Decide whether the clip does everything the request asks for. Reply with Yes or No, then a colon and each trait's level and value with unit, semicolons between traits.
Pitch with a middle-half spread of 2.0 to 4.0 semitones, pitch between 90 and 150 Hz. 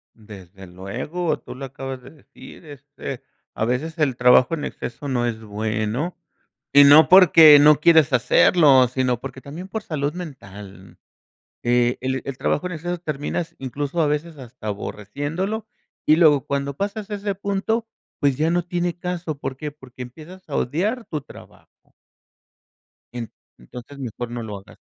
No: average, 5.3 semitones; medium, 140 Hz